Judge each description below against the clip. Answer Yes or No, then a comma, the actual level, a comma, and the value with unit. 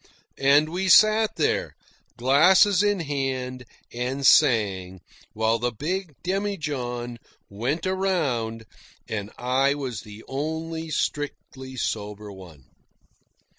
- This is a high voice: No, low, 135 Hz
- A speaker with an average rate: No, slow, 100 wpm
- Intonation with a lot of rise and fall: Yes, wide, 6.1 semitones